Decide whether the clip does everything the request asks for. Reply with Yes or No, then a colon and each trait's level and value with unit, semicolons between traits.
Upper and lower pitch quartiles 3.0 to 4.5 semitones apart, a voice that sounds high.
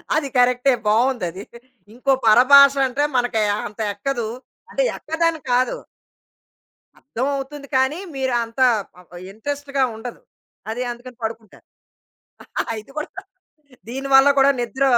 Yes: average, 3.3 semitones; very high, 260 Hz